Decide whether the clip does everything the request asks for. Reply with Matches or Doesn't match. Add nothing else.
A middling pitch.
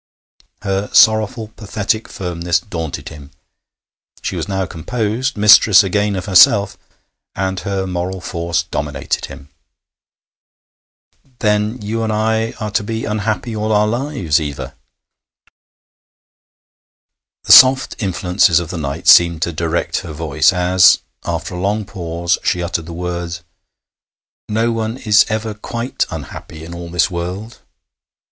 Doesn't match